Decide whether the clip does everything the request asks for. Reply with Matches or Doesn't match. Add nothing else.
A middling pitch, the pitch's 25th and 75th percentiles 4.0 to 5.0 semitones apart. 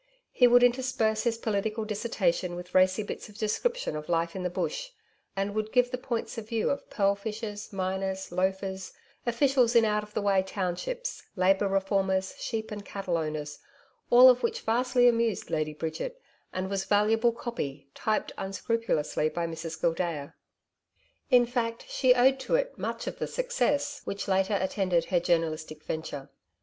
Doesn't match